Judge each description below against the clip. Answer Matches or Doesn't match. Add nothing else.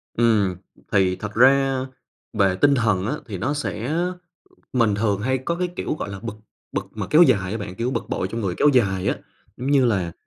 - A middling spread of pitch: Matches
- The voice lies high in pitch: Doesn't match